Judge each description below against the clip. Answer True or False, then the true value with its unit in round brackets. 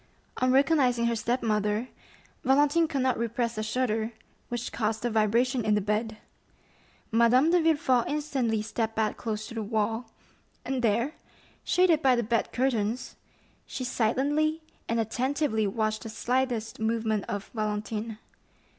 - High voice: True (235 Hz)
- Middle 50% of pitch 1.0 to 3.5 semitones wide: True (3.1 semitones)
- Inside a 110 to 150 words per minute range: True (145 wpm)